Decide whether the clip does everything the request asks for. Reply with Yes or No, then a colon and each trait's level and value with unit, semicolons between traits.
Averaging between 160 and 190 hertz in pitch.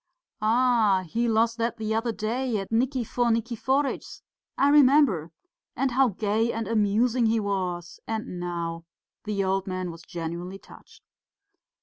No: high, 220 Hz